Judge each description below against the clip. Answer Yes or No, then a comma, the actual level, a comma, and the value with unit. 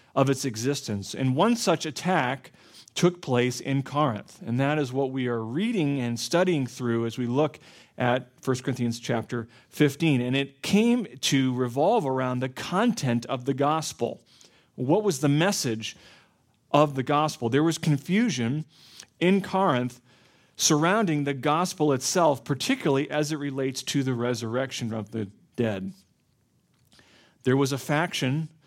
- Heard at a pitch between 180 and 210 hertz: No, low, 135 Hz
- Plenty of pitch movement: No, average, 3.7 semitones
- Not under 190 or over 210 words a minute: No, average, 145 wpm